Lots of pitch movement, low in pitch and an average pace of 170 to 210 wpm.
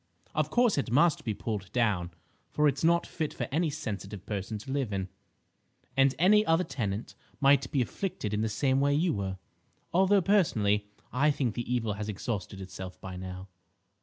Yes: wide, 6.7 semitones; low, 125 Hz; average, 180 wpm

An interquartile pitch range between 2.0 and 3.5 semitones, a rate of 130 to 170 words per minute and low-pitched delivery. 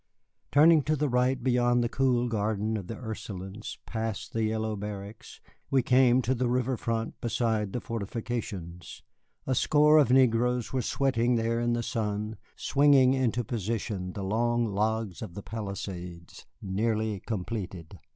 Yes: average, 3.1 semitones; average, 150 wpm; low, 115 Hz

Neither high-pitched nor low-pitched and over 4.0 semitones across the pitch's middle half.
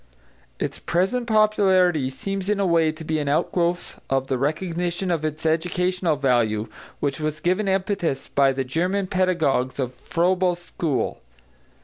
Yes: medium, 170 Hz; average, 4.6 semitones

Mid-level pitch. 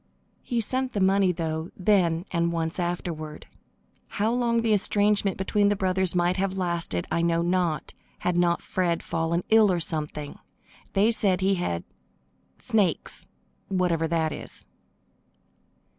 Yes: medium, 180 Hz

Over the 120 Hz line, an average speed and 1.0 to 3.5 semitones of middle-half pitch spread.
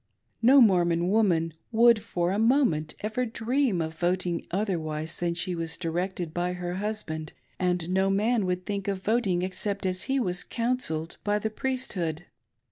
No: medium, 185 Hz; average, 160 wpm; average, 4.1 semitones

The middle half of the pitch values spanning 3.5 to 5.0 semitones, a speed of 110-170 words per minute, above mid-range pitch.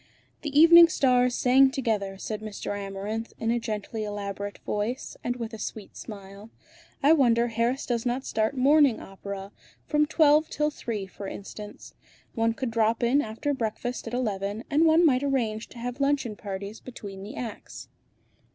Yes: average, 4.3 semitones; average, 165 wpm; high, 230 Hz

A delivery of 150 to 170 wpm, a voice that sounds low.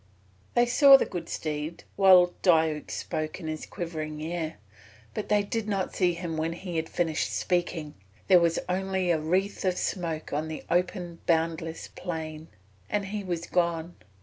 No: average, 165 wpm; medium, 170 Hz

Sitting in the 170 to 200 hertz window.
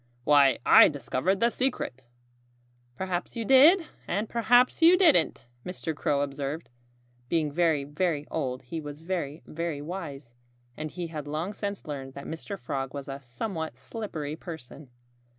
No: medium, 155 Hz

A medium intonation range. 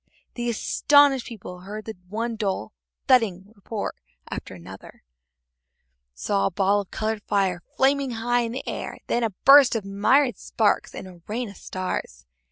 Yes: average, 4.3 semitones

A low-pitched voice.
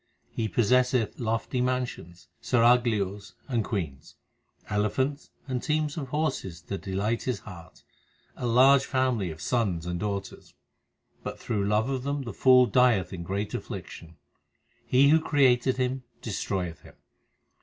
Yes: low, 115 Hz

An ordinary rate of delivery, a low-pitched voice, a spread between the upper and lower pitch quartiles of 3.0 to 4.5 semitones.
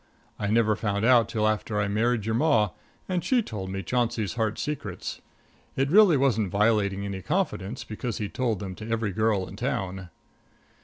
Yes: average, 175 wpm; low, 110 Hz; average, 3.4 semitones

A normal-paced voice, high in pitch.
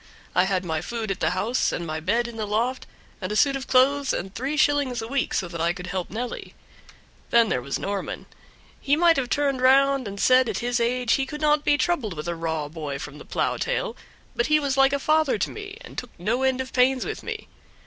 No: fast, 240 wpm; high, 245 Hz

